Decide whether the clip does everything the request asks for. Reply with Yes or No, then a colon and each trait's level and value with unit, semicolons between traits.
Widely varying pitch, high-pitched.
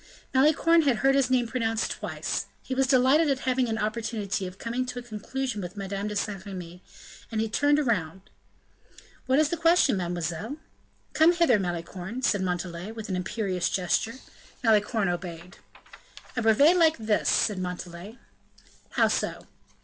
Yes: wide, 5.7 semitones; high, 220 Hz